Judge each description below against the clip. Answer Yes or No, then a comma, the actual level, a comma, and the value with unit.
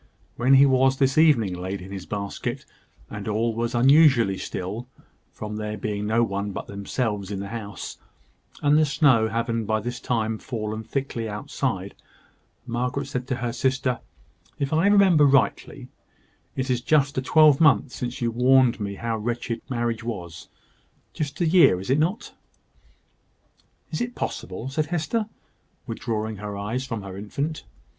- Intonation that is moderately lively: Yes, average, 4.3 semitones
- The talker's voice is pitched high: No, low, 120 Hz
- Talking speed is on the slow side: No, average, 155 wpm